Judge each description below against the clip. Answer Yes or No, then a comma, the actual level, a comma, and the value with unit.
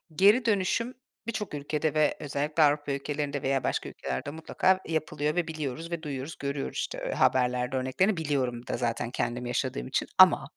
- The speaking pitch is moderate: Yes, medium, 145 Hz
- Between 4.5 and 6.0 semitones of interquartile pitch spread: No, average, 3.8 semitones